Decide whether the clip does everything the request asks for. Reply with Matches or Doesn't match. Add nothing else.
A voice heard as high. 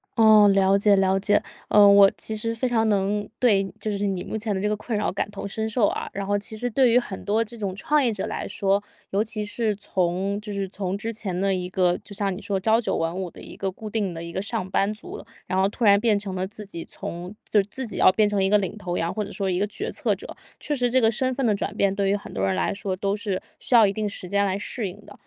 Matches